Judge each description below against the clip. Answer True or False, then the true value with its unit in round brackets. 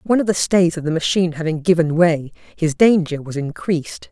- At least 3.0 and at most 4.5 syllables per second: False (5.6 syllables/s)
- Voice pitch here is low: False (170 Hz)